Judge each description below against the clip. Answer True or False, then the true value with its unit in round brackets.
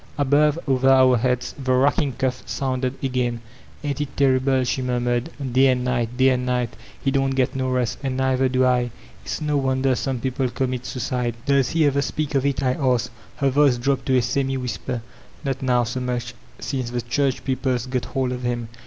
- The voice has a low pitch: True (130 Hz)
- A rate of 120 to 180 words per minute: False (200 wpm)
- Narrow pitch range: True (1.4 semitones)